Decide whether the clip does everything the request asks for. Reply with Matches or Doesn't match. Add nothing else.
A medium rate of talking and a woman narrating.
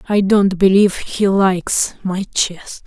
Matches